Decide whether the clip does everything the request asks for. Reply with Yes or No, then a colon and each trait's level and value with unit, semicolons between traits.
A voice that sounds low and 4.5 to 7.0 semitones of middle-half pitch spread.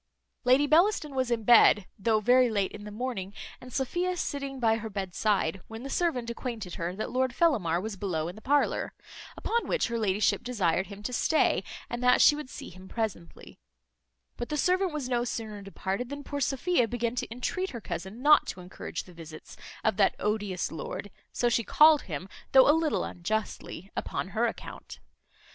No: high, 230 Hz; average, 5.2 semitones